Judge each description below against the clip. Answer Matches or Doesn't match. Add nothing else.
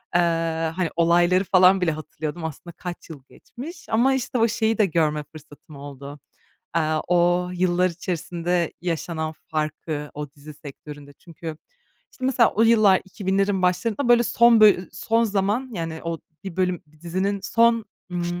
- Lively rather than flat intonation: Doesn't match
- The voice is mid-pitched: Matches